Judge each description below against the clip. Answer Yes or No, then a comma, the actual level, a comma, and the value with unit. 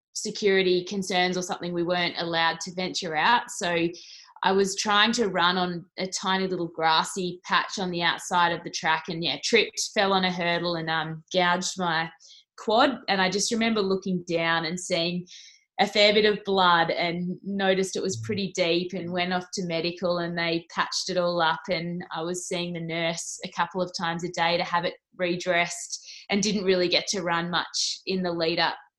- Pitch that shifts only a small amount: Yes, narrow, 2.0 semitones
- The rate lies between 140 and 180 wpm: No, average, 200 wpm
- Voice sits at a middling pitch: Yes, medium, 180 Hz